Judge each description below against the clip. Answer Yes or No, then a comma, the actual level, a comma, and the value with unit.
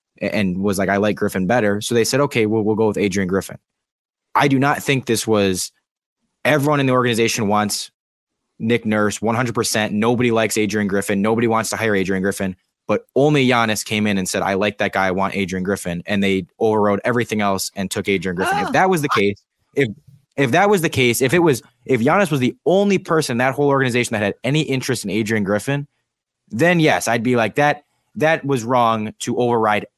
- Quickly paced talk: Yes, fast, 220 wpm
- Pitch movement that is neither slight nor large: Yes, average, 4.6 semitones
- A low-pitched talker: Yes, low, 115 Hz